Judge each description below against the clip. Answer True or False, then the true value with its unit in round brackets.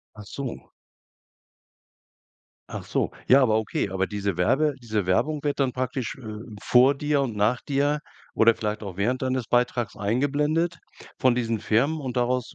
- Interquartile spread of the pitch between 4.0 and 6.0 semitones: True (4.3 semitones)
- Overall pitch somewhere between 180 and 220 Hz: False (125 Hz)